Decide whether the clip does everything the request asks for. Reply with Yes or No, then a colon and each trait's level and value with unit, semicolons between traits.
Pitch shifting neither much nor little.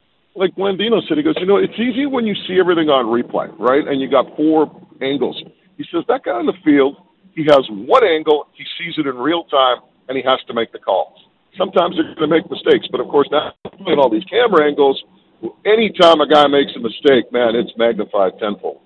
No: wide, 6.1 semitones